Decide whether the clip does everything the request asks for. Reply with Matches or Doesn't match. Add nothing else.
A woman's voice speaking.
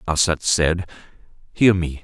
Doesn't match